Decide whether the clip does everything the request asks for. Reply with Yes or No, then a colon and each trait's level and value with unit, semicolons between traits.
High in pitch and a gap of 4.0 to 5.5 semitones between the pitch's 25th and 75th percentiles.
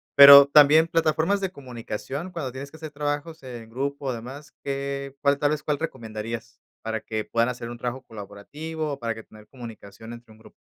No: low, 135 Hz; average, 4.3 semitones